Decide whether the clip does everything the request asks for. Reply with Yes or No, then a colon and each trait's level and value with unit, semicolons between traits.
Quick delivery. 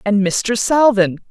No: average, 140 wpm